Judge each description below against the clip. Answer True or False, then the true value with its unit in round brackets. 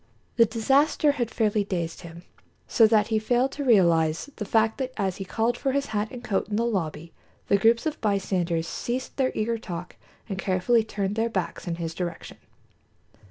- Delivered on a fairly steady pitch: False (4.4 semitones)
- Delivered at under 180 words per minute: False (190 wpm)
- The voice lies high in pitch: True (215 Hz)